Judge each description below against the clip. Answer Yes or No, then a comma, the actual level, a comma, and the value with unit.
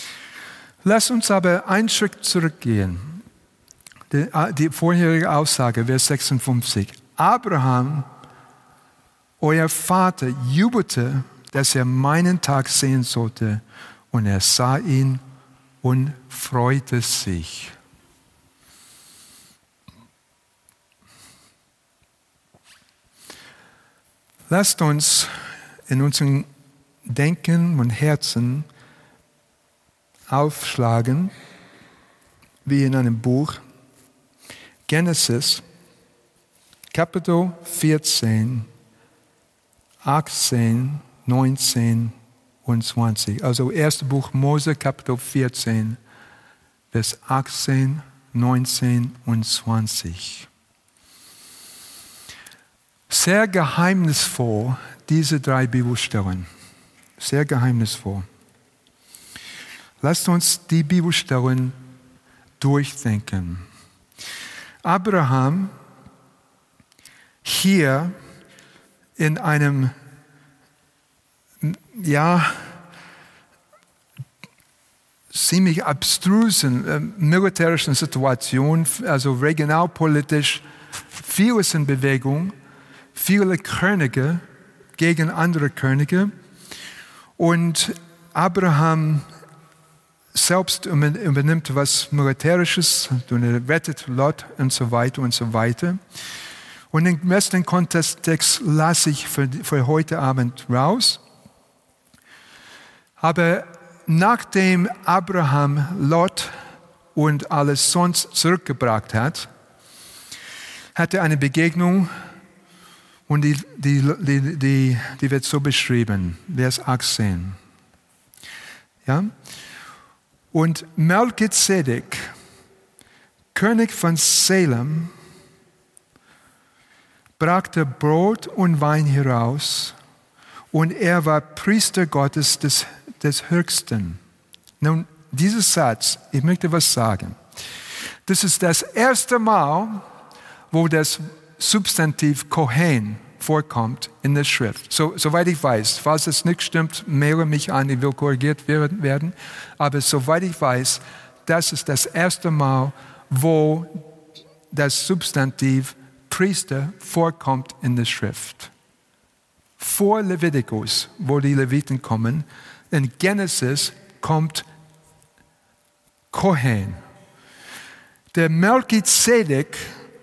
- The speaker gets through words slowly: Yes, slow, 80 wpm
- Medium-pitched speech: Yes, medium, 150 Hz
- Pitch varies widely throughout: No, average, 4.7 semitones